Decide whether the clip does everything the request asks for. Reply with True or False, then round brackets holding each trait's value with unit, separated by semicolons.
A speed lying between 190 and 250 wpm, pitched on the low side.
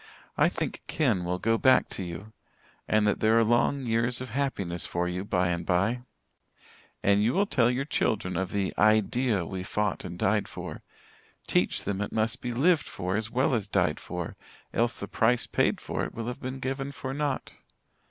True (195 wpm; 110 Hz)